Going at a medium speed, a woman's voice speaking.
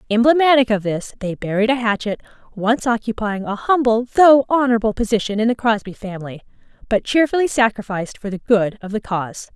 Yes: average, 170 wpm; female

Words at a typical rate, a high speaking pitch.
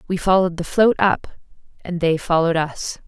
No: average, 175 wpm; medium, 175 Hz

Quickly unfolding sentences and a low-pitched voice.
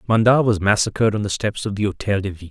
Yes: fast, 265 wpm; low, 105 Hz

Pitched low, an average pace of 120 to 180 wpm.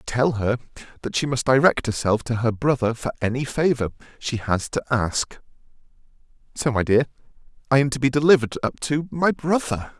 Yes: low, 130 Hz; average, 170 wpm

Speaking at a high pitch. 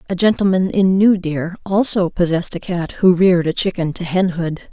No: medium, 180 Hz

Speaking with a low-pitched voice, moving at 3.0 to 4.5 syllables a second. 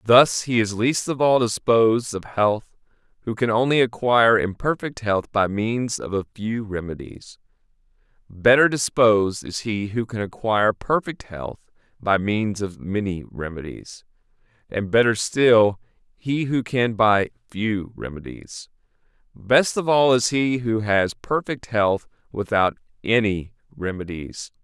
Yes: low, 110 Hz; 4.1 syllables/s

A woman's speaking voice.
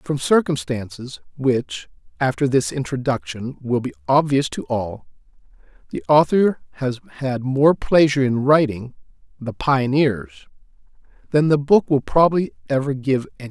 No: male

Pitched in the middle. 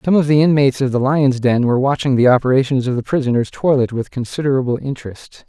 No: low, 130 Hz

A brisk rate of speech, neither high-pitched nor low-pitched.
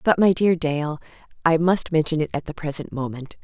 Yes: fast, 210 wpm; medium, 160 Hz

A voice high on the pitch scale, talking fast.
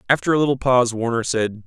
No: low, 120 Hz; fast, 215 wpm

